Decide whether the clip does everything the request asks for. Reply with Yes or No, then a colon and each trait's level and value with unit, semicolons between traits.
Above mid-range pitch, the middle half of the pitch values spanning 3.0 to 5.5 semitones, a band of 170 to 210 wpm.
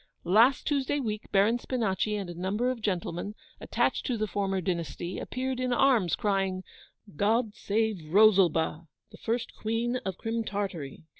No: high, 210 Hz; average, 3.8 semitones; average, 150 wpm